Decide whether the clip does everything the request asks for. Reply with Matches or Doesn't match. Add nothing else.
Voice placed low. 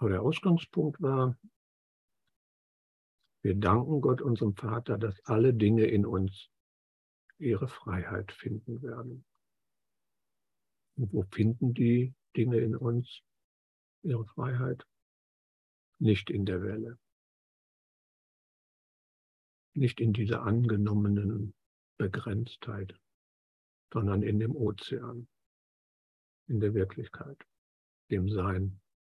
Matches